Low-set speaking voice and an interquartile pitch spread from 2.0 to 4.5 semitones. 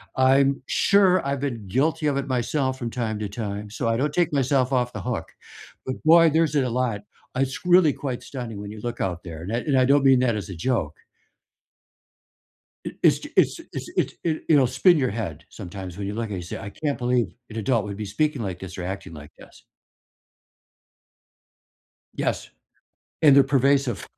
No: low, 125 Hz; average, 5.2 semitones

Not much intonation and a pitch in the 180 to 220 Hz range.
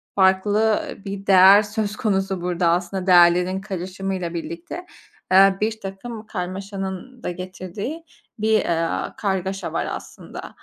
Yes: narrow, 2.2 semitones; high, 190 Hz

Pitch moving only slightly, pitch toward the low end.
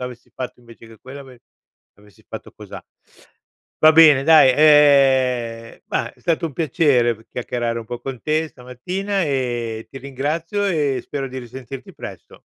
No: average, 4.0 semitones; low, 130 Hz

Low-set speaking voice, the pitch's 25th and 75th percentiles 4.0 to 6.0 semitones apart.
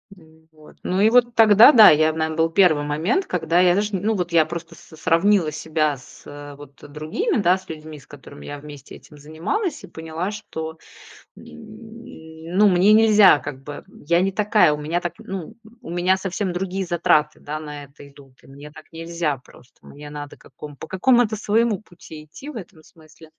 No: medium, 165 Hz; average, 4.4 semitones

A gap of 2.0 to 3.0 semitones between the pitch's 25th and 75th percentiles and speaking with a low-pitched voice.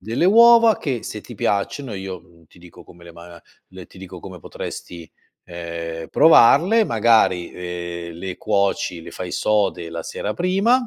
No: wide, 5.5 semitones; very low, 95 Hz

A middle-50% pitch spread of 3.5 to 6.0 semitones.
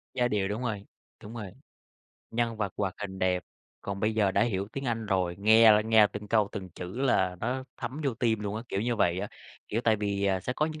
No: average, 2.9 semitones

